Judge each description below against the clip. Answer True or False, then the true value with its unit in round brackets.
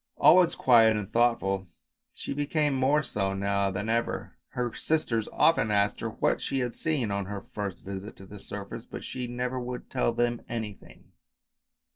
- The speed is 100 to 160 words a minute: False (170 wpm)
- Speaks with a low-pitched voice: True (115 Hz)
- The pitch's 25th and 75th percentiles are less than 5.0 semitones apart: True (3.9 semitones)